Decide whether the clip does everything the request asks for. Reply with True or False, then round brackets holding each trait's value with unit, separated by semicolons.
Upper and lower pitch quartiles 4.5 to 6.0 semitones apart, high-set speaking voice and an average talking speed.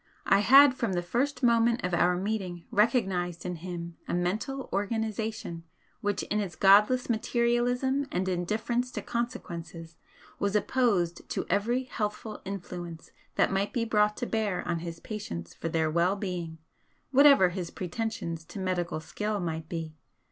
True (4.8 semitones; 200 Hz; 150 wpm)